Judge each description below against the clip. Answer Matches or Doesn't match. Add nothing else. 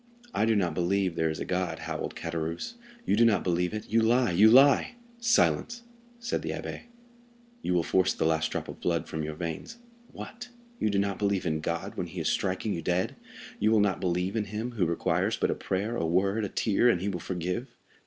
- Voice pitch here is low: Matches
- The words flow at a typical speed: Doesn't match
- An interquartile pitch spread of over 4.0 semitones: Matches